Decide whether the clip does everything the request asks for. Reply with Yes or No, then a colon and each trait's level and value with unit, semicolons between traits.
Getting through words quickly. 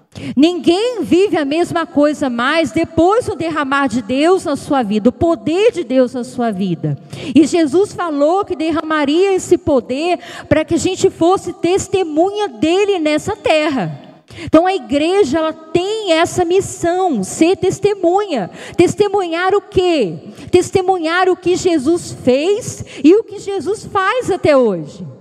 No: average, 145 wpm